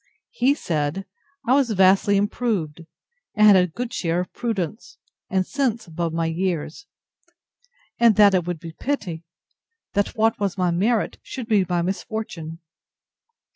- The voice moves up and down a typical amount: Yes, average, 4.7 semitones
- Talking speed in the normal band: Yes, average, 145 wpm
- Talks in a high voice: Yes, high, 195 Hz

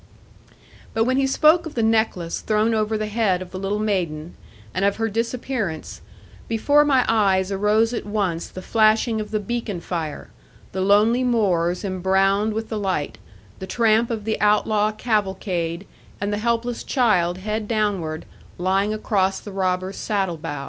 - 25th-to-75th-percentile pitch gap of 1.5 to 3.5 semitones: Yes, average, 3.0 semitones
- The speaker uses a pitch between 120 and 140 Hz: No, high, 210 Hz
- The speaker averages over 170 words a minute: No, average, 160 wpm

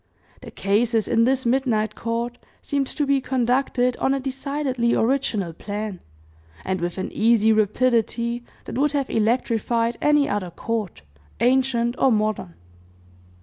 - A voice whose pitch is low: No, high, 235 Hz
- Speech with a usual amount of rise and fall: Yes, average, 3.4 semitones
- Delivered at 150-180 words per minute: No, slow, 135 wpm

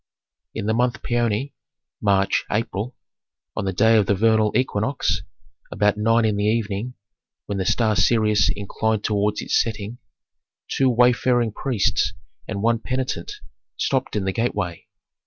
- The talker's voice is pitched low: Yes, low, 110 Hz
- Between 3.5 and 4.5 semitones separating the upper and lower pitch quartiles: No, narrow, 2.6 semitones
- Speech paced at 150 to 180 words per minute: No, average, 140 wpm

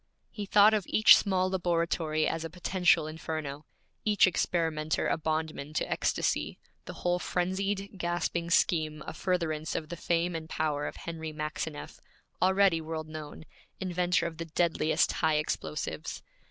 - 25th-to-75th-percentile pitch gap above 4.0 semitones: No, narrow, 2.4 semitones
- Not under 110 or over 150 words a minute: Yes, average, 145 wpm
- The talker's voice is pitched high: No, medium, 165 Hz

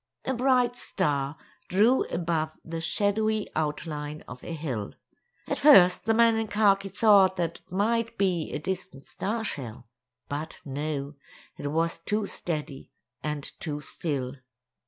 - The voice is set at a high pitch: No, medium, 170 Hz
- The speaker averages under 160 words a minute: Yes, average, 140 wpm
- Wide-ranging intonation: Yes, wide, 6.0 semitones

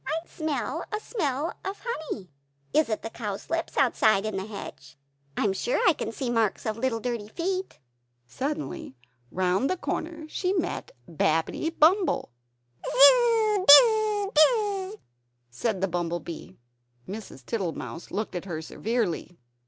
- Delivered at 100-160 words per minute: Yes, average, 145 wpm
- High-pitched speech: Yes, very high, 255 Hz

